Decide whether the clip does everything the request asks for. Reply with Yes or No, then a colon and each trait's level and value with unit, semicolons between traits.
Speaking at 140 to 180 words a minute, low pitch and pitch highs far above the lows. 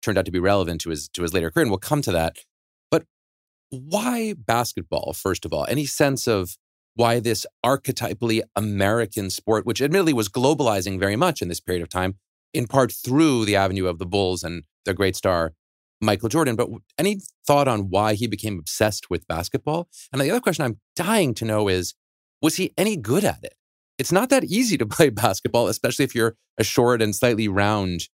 No: average, 200 wpm; low, 115 Hz; wide, 6.7 semitones